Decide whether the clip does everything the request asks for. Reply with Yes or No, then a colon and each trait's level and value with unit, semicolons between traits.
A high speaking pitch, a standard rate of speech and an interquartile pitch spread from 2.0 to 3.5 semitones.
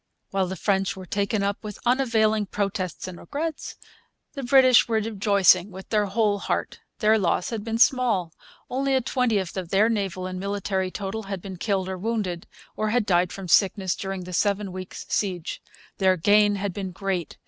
Yes: high, 200 Hz; average, 180 wpm; average, 2.7 semitones